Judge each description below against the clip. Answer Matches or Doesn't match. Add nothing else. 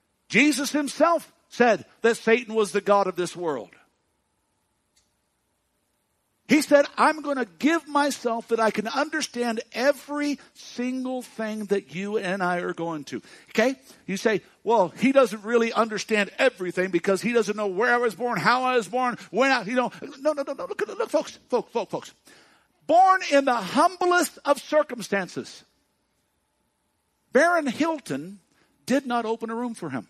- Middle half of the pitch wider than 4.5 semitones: Matches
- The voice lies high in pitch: Matches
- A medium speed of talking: Matches